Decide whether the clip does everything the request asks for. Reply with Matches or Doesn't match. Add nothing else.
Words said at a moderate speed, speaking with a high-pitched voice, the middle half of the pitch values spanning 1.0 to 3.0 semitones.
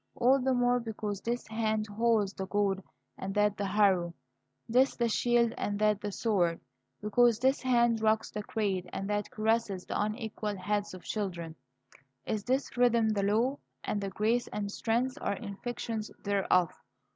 Matches